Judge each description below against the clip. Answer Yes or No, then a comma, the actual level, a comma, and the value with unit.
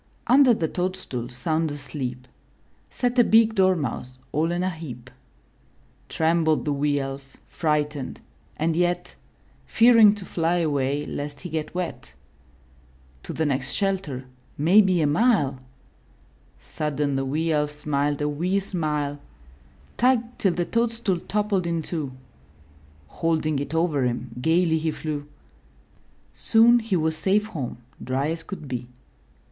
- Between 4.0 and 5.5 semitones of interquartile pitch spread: Yes, average, 4.5 semitones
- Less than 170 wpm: Yes, slow, 135 wpm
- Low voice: No, medium, 160 Hz